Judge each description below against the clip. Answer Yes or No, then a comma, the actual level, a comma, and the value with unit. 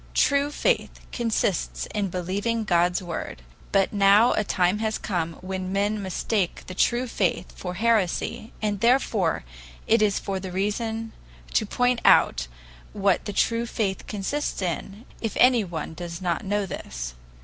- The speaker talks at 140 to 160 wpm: Yes, average, 150 wpm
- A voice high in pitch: Yes, high, 200 Hz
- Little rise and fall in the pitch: No, average, 3.6 semitones